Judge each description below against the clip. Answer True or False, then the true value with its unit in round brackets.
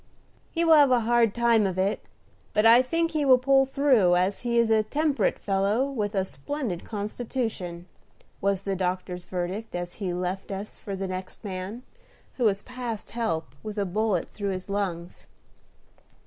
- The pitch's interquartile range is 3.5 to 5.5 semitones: True (4.5 semitones)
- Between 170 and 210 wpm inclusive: True (175 wpm)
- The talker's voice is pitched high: True (210 Hz)